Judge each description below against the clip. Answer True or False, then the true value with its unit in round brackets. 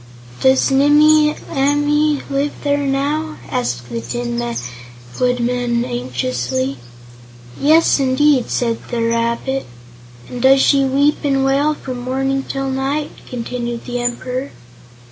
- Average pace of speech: False (115 wpm)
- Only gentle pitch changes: False (3.2 semitones)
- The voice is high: True (265 Hz)